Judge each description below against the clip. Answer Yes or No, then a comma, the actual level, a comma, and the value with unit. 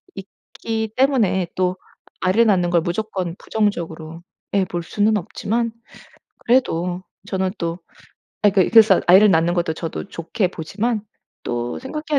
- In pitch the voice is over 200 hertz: No, high, 190 Hz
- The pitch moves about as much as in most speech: Yes, average, 4.3 semitones